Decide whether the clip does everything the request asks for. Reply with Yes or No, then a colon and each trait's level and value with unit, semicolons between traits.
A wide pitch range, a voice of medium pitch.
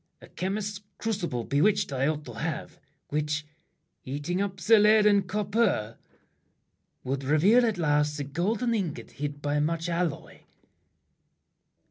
Yes: wide, 6.0 semitones; medium, 165 Hz